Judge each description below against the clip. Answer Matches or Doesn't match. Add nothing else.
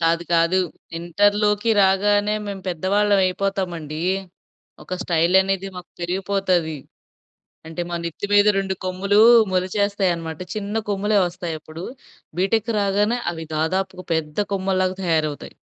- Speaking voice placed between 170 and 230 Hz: Matches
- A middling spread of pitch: Matches